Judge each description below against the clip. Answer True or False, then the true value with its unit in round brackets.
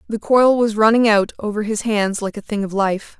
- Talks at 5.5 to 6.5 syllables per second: False (5.1 syllables/s)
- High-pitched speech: True (215 Hz)